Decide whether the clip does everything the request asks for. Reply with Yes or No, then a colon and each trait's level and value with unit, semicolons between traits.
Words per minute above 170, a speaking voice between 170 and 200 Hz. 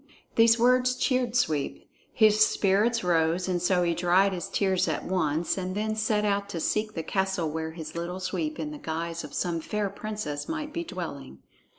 Yes: average, 190 wpm; high, 190 Hz